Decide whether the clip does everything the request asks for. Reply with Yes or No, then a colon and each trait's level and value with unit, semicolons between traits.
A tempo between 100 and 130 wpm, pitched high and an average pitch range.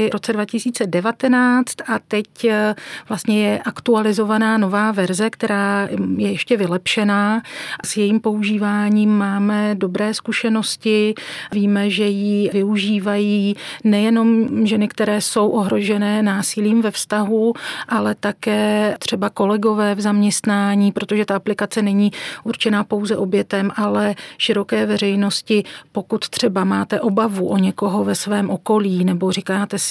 No: average, 120 wpm; high, 210 Hz; narrow, 1.3 semitones